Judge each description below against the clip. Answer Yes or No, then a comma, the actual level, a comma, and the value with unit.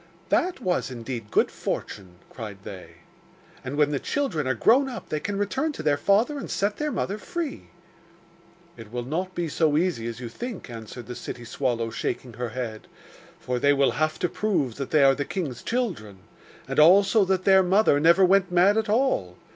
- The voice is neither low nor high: Yes, medium, 155 Hz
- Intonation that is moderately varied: No, wide, 8.4 semitones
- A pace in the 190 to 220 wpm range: Yes, average, 195 wpm